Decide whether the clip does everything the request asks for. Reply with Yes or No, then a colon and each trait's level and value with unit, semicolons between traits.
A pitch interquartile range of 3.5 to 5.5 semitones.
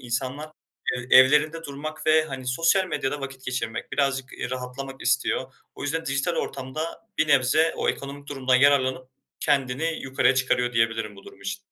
No: narrow, 2.6 semitones